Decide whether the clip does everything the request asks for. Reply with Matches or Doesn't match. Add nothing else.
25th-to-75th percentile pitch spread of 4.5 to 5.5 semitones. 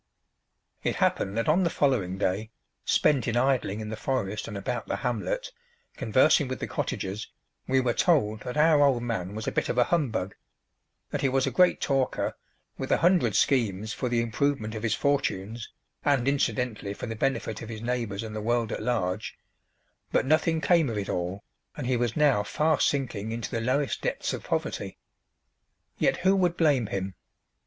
Matches